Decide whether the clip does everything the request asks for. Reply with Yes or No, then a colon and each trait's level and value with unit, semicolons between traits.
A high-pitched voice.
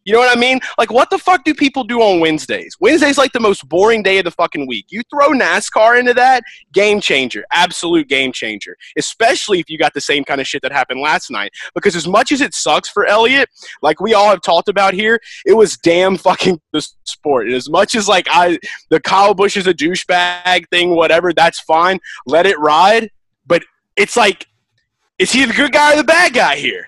Yes: high, 200 Hz